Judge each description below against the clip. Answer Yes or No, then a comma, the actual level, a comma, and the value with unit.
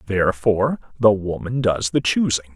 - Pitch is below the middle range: Yes, low, 105 Hz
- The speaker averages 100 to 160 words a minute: Yes, average, 140 wpm